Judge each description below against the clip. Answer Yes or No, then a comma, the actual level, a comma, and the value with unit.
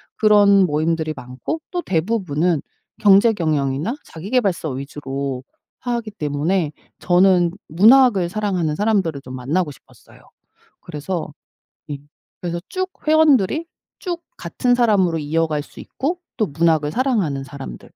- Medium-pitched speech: Yes, medium, 175 Hz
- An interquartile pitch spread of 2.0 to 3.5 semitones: No, wide, 6.3 semitones